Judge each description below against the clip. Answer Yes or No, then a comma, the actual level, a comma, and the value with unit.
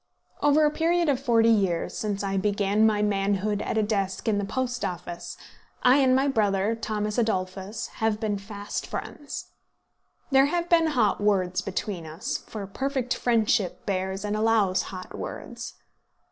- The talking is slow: No, average, 160 wpm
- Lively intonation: No, average, 3.9 semitones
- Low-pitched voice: No, high, 210 Hz